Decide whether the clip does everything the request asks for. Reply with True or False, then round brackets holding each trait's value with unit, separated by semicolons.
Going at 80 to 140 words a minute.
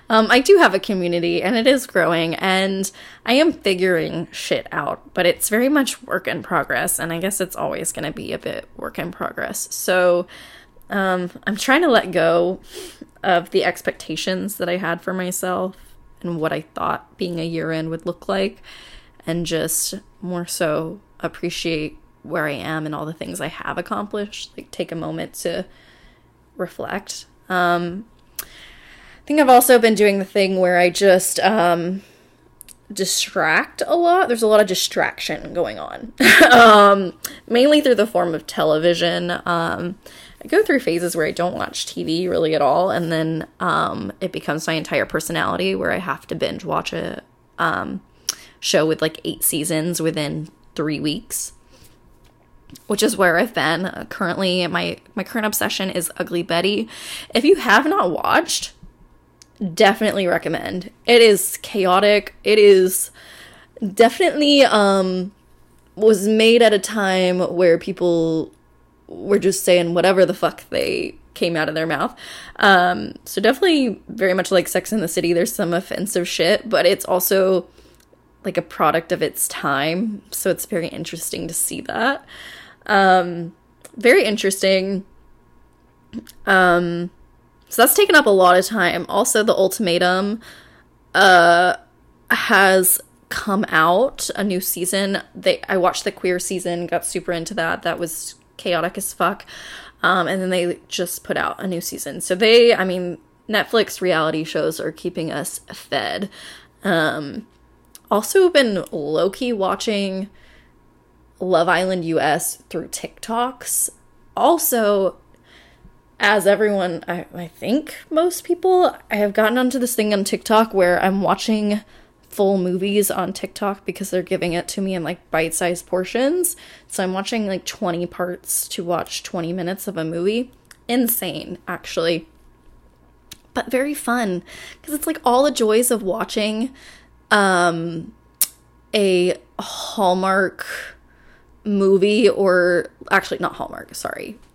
False (150 wpm)